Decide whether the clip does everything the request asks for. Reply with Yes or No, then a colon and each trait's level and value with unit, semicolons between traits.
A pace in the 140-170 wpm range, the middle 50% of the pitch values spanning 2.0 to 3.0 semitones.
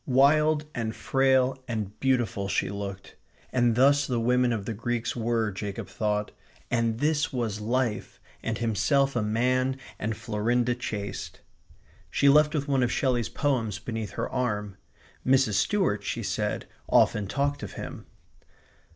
No: average, 145 wpm; average, 3.9 semitones